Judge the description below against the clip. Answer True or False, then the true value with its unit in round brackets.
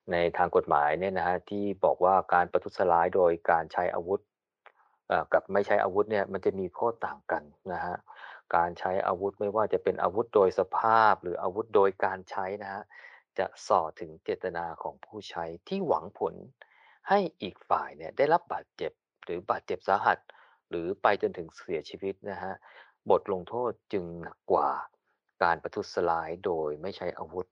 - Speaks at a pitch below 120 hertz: True (100 Hz)